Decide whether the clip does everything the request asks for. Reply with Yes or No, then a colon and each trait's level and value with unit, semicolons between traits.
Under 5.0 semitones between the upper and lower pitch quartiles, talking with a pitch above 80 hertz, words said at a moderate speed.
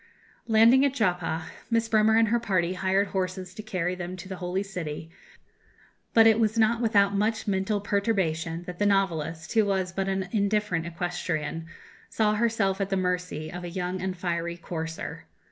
Yes: average, 3.3 semitones; high, 190 Hz; average, 175 wpm